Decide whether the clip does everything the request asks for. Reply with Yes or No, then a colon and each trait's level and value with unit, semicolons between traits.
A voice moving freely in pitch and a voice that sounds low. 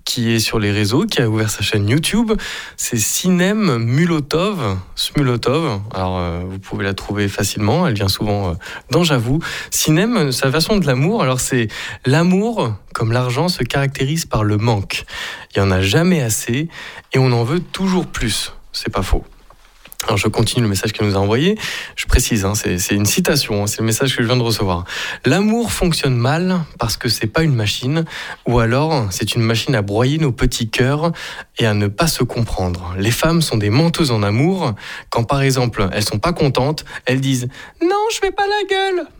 Yes: wide, 6.9 semitones; low, 125 Hz